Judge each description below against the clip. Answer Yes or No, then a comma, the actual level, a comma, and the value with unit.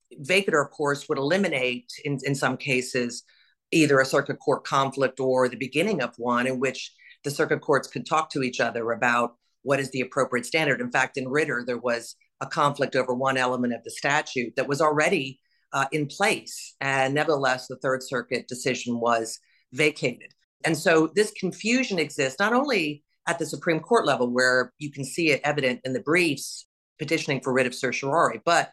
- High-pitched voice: No, low, 135 Hz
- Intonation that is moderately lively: Yes, average, 3.2 semitones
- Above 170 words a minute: Yes, average, 190 wpm